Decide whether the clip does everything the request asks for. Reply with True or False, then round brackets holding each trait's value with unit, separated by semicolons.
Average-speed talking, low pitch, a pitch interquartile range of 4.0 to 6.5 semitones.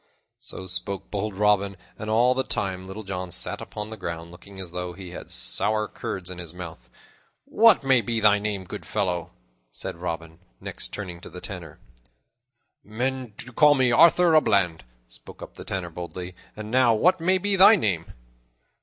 True (180 wpm; 100 Hz; 5.0 semitones)